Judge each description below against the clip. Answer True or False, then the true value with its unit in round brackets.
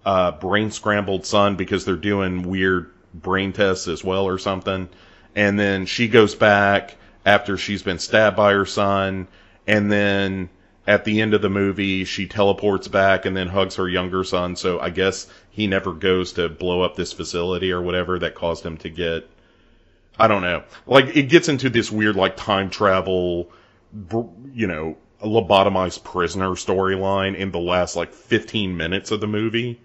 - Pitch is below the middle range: True (95 Hz)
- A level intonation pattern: True (2.0 semitones)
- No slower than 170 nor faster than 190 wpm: True (175 wpm)